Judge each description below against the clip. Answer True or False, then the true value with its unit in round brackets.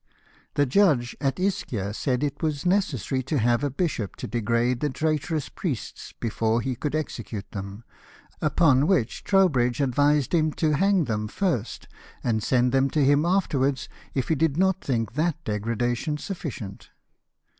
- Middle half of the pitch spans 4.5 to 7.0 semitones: True (4.8 semitones)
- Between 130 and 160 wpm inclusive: True (155 wpm)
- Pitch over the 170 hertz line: False (140 Hz)